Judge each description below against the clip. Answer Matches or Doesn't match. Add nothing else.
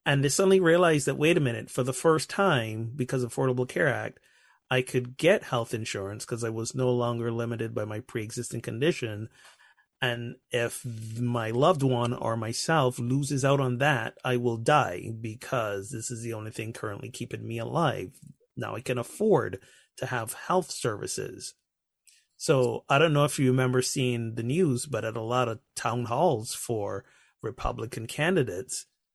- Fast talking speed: Doesn't match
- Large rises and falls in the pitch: Doesn't match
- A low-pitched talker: Matches